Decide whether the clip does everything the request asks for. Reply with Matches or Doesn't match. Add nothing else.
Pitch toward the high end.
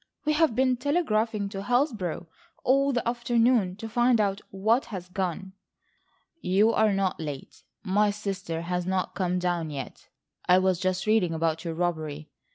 Matches